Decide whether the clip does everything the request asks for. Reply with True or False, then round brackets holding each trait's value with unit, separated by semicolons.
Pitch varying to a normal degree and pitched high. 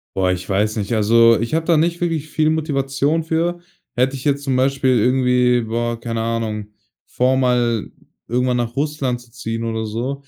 False (3.5 semitones; 125 Hz)